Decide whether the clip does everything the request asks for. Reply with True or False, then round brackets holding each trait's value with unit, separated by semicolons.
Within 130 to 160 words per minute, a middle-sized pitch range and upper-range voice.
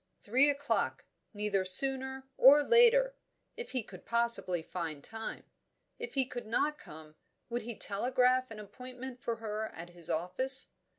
True (150 wpm; 5.0 semitones; 240 Hz)